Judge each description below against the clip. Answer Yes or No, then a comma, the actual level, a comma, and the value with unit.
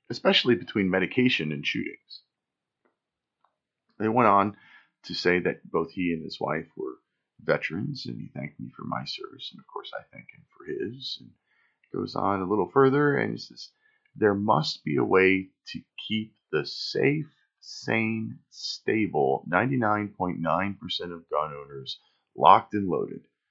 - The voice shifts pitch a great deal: Yes, wide, 6.4 semitones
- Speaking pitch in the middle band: No, low, 105 Hz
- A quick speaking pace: No, average, 155 wpm